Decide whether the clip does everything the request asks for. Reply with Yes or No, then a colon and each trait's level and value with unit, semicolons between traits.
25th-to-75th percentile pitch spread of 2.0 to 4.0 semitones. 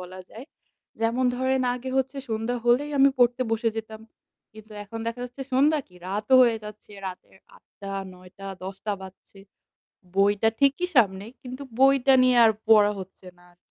No: average, 4.4 semitones